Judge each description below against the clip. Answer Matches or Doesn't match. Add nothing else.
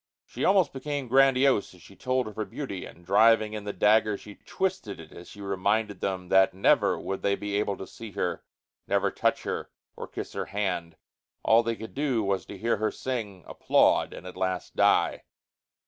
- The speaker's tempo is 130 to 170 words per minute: Doesn't match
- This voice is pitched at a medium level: Doesn't match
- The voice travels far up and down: Doesn't match